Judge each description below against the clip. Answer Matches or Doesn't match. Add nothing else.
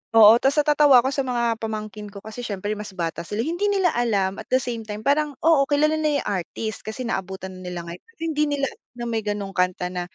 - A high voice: Matches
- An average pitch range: Doesn't match